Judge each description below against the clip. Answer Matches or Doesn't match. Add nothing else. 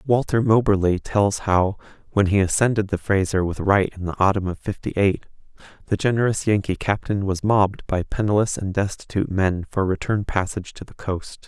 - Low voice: Matches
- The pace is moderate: Matches